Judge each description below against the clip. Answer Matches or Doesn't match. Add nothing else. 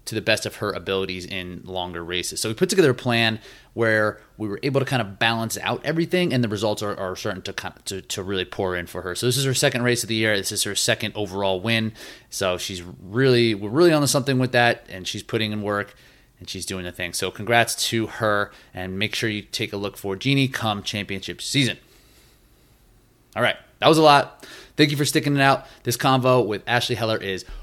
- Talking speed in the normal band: Doesn't match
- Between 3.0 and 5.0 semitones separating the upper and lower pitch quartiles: Matches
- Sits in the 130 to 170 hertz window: Doesn't match